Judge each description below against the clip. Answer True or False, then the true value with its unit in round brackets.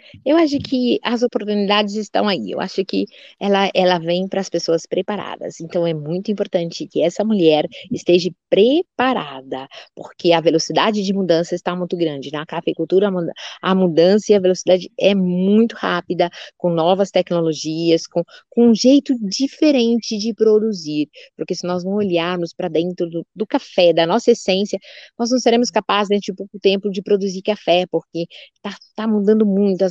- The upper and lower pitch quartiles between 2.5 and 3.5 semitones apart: False (3.9 semitones)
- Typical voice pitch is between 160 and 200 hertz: True (190 Hz)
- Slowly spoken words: False (175 wpm)